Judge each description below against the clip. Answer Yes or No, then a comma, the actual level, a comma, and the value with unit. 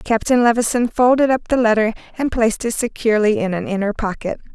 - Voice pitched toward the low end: No, high, 225 Hz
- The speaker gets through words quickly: No, average, 185 wpm